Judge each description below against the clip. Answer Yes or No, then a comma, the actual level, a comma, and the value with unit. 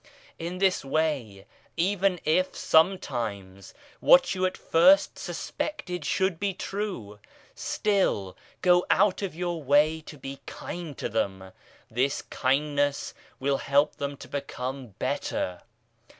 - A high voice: No, medium, 150 Hz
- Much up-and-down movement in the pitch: Yes, wide, 5.9 semitones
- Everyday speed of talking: No, slow, 120 wpm